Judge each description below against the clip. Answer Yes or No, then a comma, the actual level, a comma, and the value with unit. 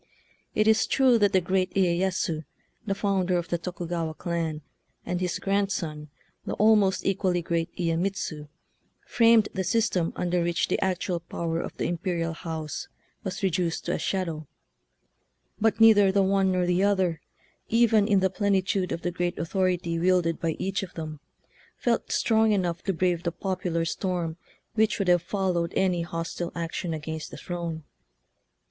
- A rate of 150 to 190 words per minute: Yes, average, 160 wpm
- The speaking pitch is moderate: Yes, medium, 180 Hz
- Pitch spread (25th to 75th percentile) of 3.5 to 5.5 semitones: No, narrow, 2.6 semitones